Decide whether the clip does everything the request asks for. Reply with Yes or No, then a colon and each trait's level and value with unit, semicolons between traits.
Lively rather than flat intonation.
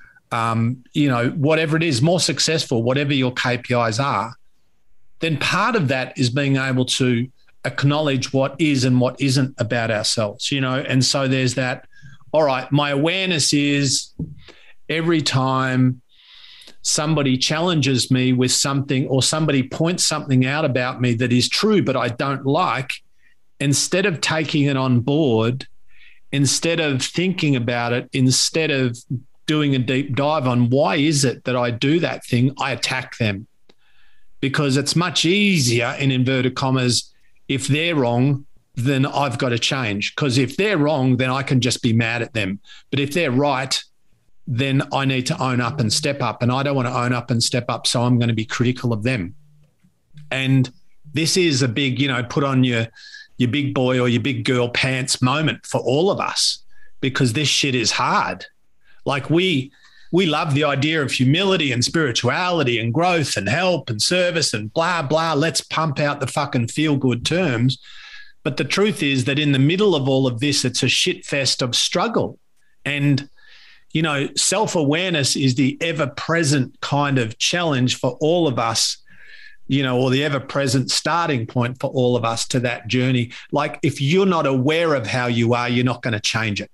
No: average, 3.3 semitones